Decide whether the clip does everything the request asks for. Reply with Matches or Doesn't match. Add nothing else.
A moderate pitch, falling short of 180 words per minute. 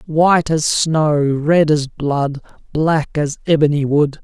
Matches